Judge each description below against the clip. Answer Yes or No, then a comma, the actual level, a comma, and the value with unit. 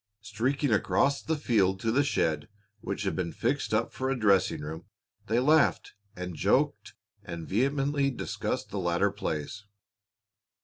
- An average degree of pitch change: No, wide, 6.9 semitones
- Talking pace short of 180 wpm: Yes, average, 145 wpm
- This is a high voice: No, low, 105 Hz